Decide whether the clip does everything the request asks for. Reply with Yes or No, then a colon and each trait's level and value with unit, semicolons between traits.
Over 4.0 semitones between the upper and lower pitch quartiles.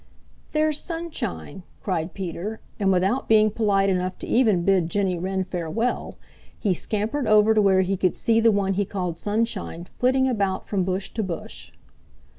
No: average, 3.2 semitones